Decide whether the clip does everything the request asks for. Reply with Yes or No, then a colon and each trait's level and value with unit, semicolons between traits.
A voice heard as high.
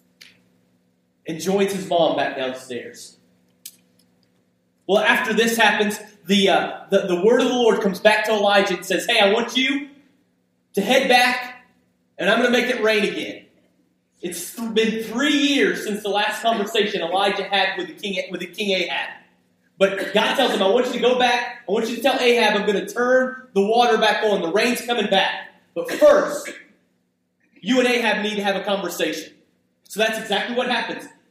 Yes: high, 210 Hz